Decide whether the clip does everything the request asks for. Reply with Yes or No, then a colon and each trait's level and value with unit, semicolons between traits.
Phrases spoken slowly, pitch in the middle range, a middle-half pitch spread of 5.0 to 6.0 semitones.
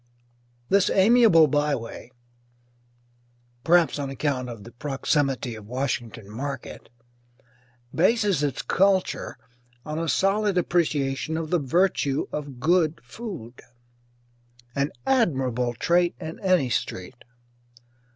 Yes: slow, 100 wpm; medium, 150 Hz; wide, 5.6 semitones